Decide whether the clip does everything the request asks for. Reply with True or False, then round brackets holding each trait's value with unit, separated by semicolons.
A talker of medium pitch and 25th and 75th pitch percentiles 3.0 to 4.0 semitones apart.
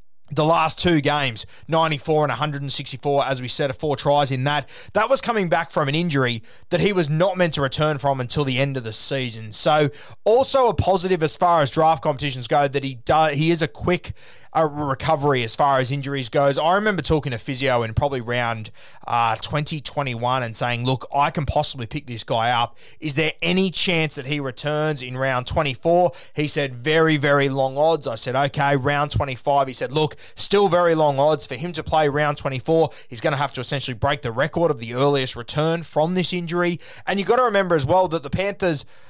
True (145 Hz; 3.4 semitones)